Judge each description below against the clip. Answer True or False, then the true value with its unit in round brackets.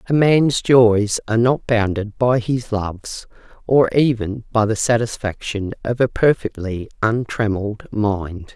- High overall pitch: False (115 Hz)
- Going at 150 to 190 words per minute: False (135 wpm)